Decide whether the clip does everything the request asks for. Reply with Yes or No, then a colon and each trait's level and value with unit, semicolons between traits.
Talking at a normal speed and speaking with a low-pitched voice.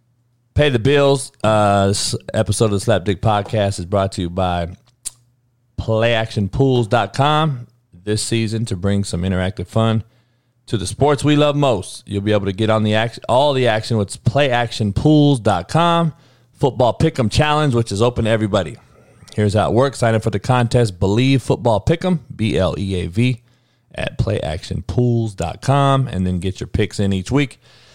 Yes: average, 160 wpm; low, 115 Hz